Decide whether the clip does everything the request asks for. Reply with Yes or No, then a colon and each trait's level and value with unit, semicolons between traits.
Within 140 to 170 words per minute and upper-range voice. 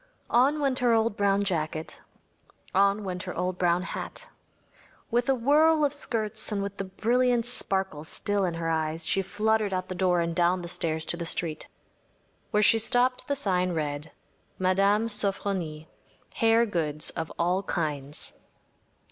Yes: average, 160 wpm; high, 195 Hz